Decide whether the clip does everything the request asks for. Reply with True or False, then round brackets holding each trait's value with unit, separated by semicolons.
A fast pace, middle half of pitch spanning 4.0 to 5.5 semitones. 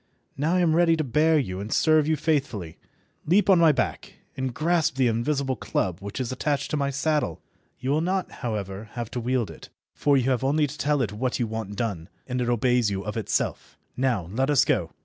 True (220 wpm; 5.2 semitones)